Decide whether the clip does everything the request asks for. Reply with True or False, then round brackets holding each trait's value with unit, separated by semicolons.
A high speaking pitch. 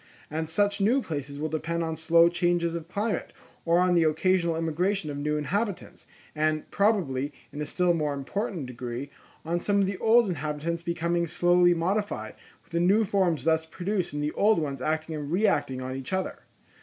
False (170 Hz)